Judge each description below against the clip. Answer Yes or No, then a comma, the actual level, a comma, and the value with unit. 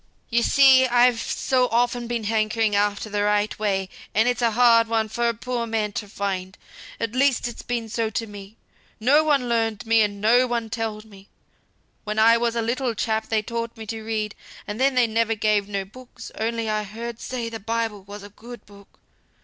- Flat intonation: Yes, narrow, 2.0 semitones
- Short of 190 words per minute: No, fast, 205 wpm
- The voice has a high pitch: Yes, high, 225 Hz